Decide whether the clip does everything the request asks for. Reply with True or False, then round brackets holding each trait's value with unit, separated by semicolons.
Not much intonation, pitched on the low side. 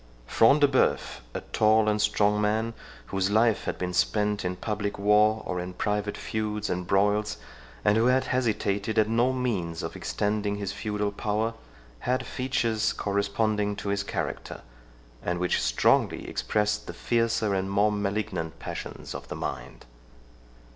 True (1.6 semitones; 105 Hz)